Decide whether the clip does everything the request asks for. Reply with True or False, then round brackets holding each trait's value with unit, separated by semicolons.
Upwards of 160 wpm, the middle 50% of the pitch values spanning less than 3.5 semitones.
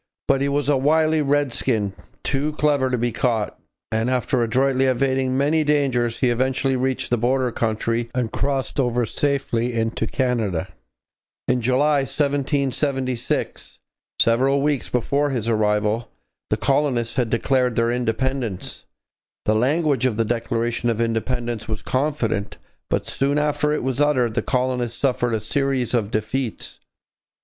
False (140 wpm; 2.9 semitones)